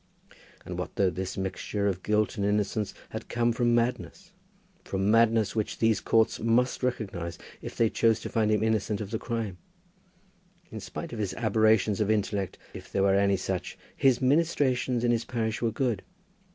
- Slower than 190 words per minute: Yes, average, 180 wpm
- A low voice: Yes, low, 110 Hz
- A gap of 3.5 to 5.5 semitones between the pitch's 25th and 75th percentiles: No, average, 2.8 semitones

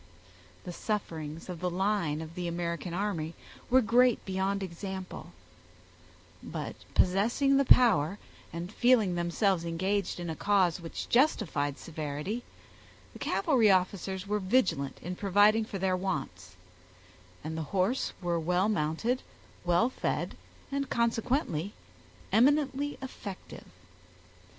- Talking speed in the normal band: No, slow, 120 wpm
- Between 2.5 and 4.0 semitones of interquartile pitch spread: No, average, 4.7 semitones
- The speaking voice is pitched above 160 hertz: Yes, high, 190 Hz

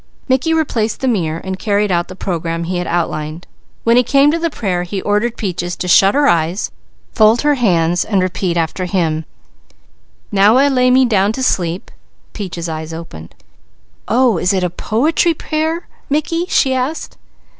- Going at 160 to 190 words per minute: Yes, average, 175 wpm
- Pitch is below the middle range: No, high, 200 Hz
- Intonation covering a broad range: Yes, wide, 6.8 semitones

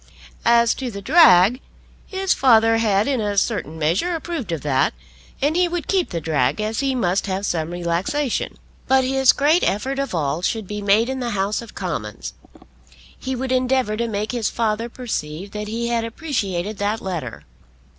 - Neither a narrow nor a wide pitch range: No, wide, 6.0 semitones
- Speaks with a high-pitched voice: Yes, high, 220 Hz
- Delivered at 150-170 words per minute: No, average, 180 wpm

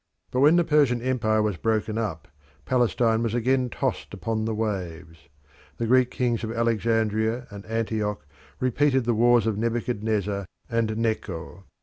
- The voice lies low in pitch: Yes, low, 115 Hz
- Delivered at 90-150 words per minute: Yes, average, 145 wpm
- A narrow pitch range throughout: Yes, narrow, 2.2 semitones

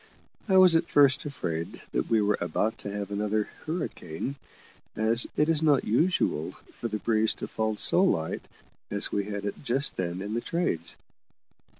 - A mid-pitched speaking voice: No, low, 110 Hz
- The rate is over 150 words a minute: Yes, average, 175 wpm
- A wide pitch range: Yes, wide, 6.3 semitones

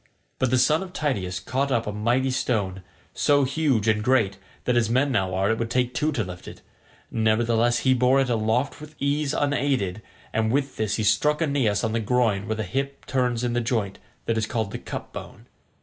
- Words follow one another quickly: Yes, fast, 210 wpm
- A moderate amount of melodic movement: Yes, average, 3.7 semitones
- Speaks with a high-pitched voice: No, low, 120 Hz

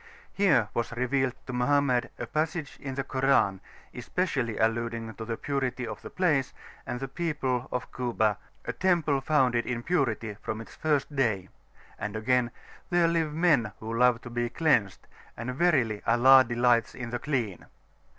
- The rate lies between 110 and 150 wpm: No, average, 165 wpm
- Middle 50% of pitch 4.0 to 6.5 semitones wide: No, average, 3.5 semitones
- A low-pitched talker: Yes, low, 125 Hz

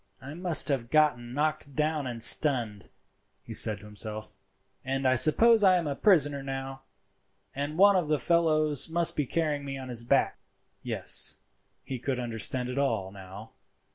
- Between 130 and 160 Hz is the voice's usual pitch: Yes, low, 135 Hz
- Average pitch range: Yes, average, 4.2 semitones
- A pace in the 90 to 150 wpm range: No, average, 170 wpm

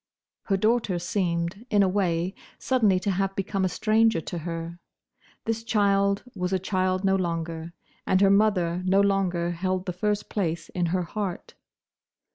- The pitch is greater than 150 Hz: Yes, high, 190 Hz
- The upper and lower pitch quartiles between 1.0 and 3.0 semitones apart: Yes, narrow, 2.5 semitones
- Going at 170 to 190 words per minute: No, average, 160 wpm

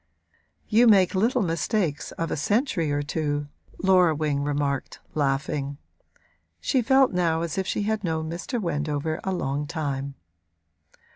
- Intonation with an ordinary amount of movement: Yes, average, 4.7 semitones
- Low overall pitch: No, medium, 160 Hz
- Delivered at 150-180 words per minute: No, average, 140 wpm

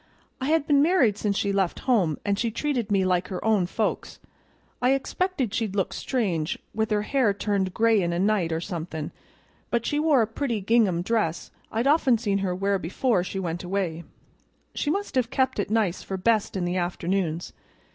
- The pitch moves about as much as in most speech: Yes, average, 4.7 semitones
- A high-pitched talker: Yes, high, 205 Hz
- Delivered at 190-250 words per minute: Yes, average, 195 wpm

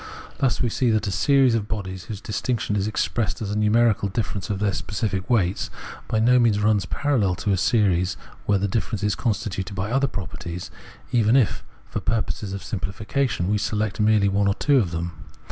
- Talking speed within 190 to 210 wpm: Yes, average, 195 wpm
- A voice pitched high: No, low, 105 Hz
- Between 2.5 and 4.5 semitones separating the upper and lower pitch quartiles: Yes, average, 2.9 semitones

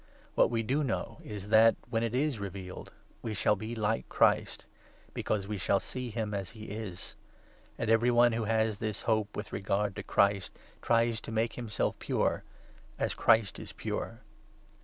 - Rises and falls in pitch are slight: Yes, narrow, 2.0 semitones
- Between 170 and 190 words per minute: Yes, average, 180 wpm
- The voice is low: Yes, low, 110 Hz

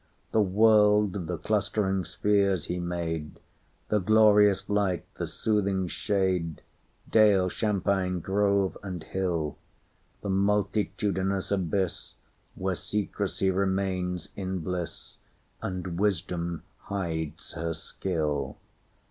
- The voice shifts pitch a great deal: No, narrow, 2.4 semitones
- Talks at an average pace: No, slow, 80 wpm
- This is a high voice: No, very low, 95 Hz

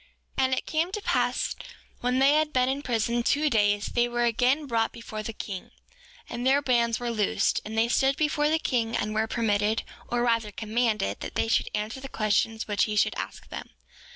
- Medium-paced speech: No, fast, 210 wpm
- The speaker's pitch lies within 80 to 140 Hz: No, high, 235 Hz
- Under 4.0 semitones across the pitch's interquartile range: Yes, average, 3.3 semitones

